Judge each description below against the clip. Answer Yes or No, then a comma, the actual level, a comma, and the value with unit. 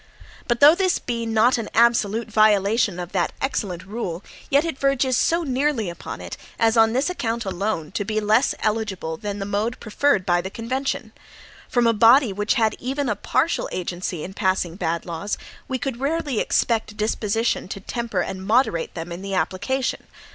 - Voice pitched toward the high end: Yes, high, 220 Hz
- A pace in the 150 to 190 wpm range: Yes, average, 185 wpm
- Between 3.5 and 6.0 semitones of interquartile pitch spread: Yes, average, 4.6 semitones